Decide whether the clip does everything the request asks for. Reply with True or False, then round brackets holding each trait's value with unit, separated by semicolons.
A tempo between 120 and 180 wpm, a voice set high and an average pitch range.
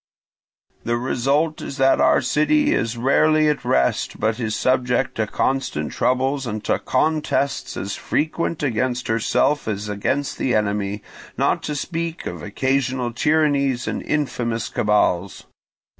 False (135 wpm; 130 Hz; 4.7 semitones)